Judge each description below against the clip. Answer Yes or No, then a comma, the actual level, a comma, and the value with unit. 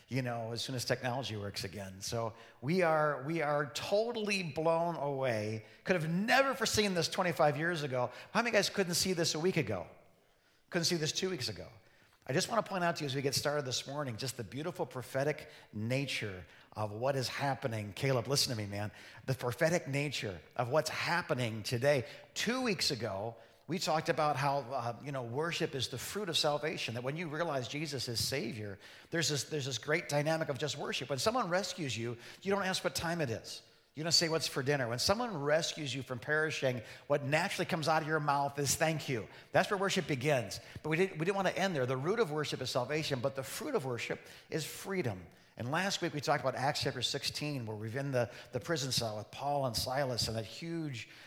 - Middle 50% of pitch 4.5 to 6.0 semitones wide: Yes, average, 5.1 semitones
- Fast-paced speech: Yes, fast, 220 wpm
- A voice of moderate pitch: Yes, medium, 145 Hz